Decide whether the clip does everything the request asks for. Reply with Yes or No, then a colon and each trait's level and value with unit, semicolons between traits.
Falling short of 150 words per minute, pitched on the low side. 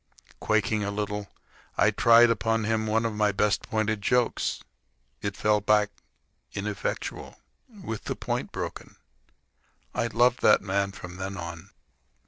Yes: slow, 135 wpm; low, 105 Hz